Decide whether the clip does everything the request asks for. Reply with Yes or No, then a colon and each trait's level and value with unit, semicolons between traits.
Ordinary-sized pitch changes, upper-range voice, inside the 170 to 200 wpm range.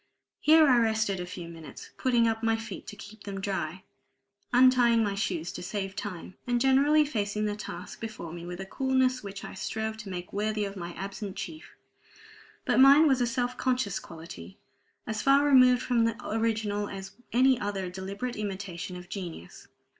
Yes: average, 4.3 semitones; high, 210 Hz; average, 180 wpm